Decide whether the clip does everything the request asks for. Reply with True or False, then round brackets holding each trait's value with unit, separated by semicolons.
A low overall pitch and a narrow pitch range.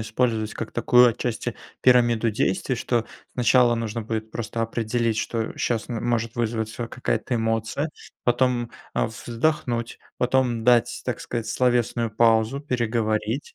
True (115 Hz; 1.6 semitones)